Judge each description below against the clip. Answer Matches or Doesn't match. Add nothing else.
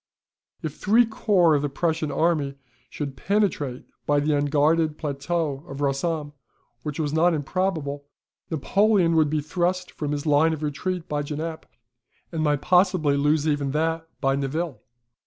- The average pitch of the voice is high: Doesn't match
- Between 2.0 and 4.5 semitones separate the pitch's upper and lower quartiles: Matches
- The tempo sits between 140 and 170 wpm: Matches